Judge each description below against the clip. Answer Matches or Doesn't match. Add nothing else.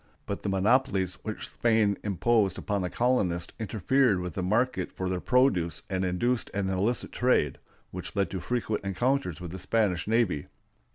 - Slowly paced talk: Doesn't match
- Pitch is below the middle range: Matches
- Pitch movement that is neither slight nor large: Matches